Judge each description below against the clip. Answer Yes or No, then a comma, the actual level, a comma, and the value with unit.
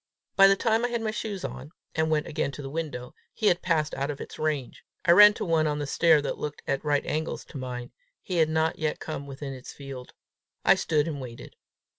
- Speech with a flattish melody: No, average, 3.4 semitones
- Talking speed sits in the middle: No, fast, 235 wpm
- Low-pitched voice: No, medium, 155 Hz